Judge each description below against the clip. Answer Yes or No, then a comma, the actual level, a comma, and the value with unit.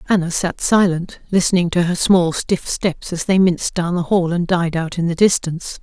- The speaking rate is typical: No, fast, 215 wpm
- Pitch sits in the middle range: Yes, medium, 175 Hz